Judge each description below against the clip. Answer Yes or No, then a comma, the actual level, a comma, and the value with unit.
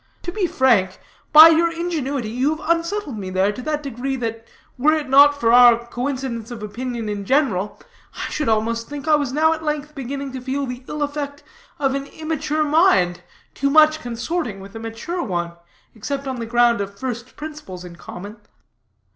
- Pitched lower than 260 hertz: No, very high, 265 Hz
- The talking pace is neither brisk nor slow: Yes, average, 190 wpm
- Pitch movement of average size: Yes, average, 5.0 semitones